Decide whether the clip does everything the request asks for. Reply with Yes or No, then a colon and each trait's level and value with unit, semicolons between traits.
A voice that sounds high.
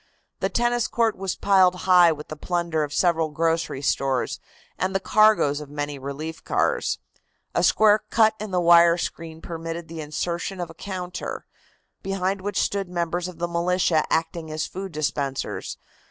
No: medium, 170 Hz